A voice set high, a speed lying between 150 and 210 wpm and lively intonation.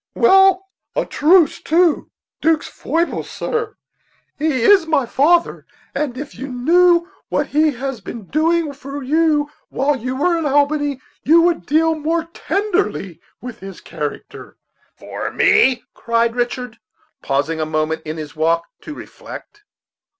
No: very high, 290 Hz; average, 140 wpm; wide, 5.7 semitones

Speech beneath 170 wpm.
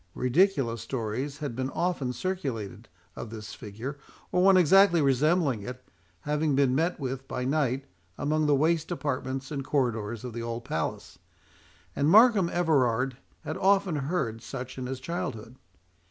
Yes: average, 150 wpm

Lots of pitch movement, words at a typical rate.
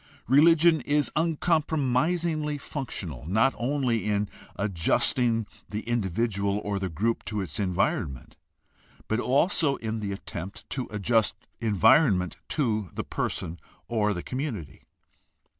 No: wide, 6.2 semitones; slow, 120 wpm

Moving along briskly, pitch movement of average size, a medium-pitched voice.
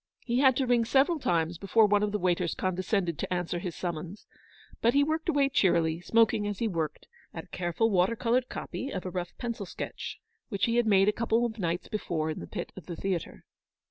No: fast, 225 wpm; average, 4.9 semitones; high, 200 Hz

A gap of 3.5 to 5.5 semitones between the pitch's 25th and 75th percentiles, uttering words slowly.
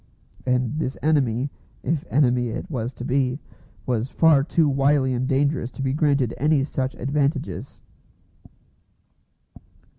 No: narrow, 2.5 semitones; slow, 125 wpm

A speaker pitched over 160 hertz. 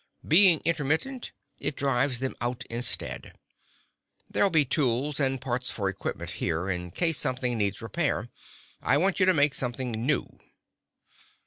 No: low, 135 Hz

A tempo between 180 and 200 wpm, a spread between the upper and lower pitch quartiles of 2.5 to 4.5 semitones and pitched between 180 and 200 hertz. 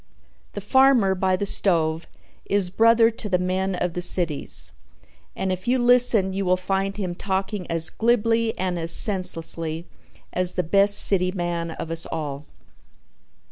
No: average, 155 wpm; average, 2.8 semitones; medium, 185 Hz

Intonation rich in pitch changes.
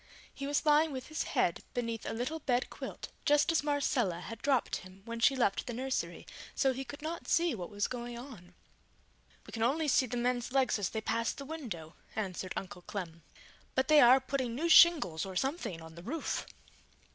Yes: wide, 5.7 semitones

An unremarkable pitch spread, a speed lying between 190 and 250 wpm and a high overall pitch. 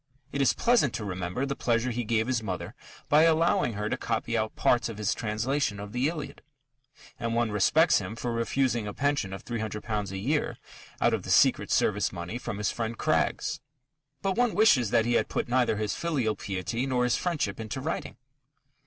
No: average, 4.4 semitones; average, 195 wpm; low, 115 Hz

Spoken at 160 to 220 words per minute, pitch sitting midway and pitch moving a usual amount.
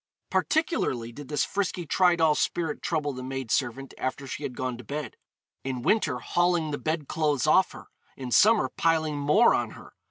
Yes: average, 180 wpm; medium, 150 Hz; average, 4.3 semitones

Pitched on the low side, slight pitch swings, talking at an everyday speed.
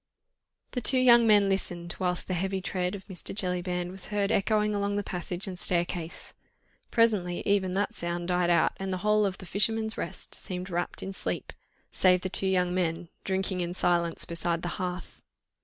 No: medium, 185 Hz; narrow, 2.2 semitones; average, 185 wpm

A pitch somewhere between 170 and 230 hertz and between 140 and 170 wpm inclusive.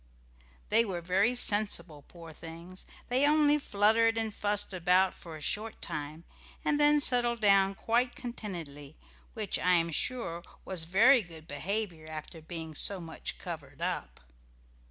Yes: high, 190 Hz; average, 145 wpm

